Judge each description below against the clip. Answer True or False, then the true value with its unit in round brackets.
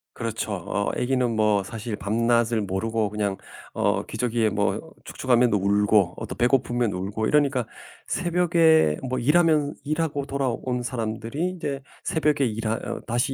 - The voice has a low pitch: True (120 Hz)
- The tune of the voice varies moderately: True (4.7 semitones)